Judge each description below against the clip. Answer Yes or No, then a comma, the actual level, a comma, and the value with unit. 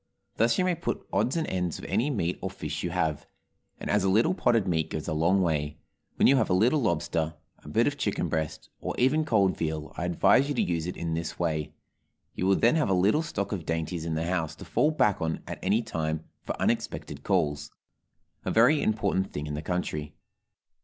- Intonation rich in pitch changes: Yes, wide, 5.8 semitones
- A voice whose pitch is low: Yes, very low, 90 Hz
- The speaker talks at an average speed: No, fast, 220 wpm